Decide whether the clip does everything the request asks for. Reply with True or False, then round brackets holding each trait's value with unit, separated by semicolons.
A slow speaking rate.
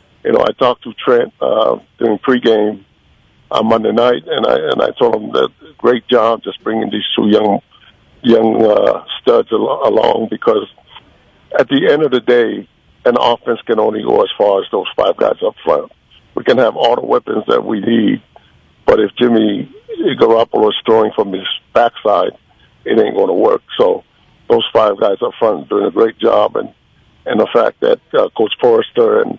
False (190 wpm)